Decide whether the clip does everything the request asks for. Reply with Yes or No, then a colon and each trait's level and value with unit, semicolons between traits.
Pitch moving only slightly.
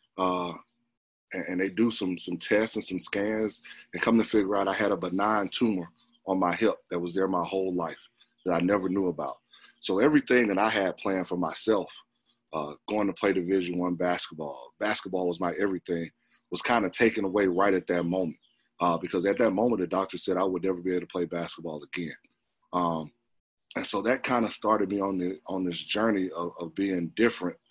Yes: narrow, 2.3 semitones